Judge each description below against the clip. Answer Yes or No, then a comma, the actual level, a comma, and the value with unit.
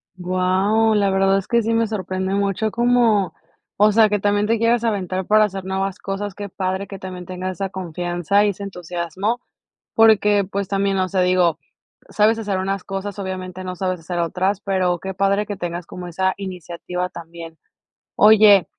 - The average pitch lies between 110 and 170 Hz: No, high, 195 Hz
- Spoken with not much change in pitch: Yes, narrow, 2.0 semitones